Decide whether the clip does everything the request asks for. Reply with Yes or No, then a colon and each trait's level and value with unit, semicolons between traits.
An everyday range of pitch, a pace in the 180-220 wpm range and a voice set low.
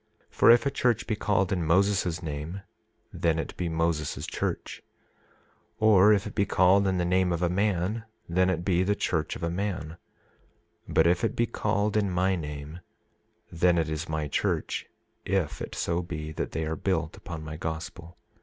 Yes: average, 3.3 semitones; average, 185 wpm; very low, 90 Hz